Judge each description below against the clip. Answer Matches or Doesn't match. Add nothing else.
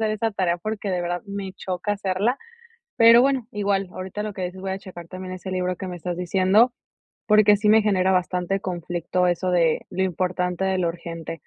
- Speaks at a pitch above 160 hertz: Matches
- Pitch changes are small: Matches